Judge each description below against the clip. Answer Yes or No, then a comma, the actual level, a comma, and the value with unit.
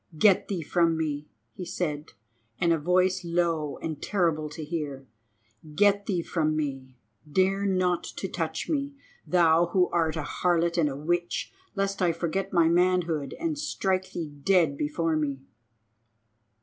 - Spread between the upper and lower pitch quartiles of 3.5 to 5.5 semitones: No, average, 3.1 semitones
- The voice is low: No, medium, 170 Hz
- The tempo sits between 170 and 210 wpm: No, average, 150 wpm